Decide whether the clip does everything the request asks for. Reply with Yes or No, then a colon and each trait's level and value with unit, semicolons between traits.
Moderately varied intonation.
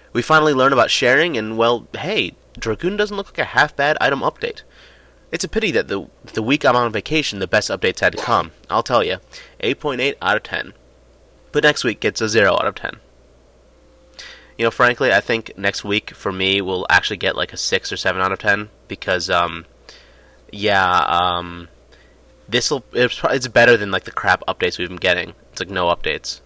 No: wide, 5.9 semitones